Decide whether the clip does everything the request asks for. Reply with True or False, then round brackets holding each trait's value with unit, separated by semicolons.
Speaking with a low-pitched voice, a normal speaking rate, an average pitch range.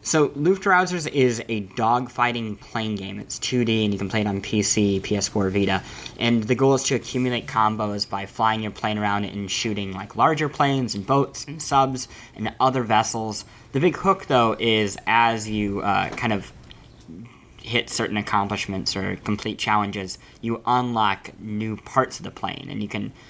True (110 Hz; 175 wpm; 3.6 semitones)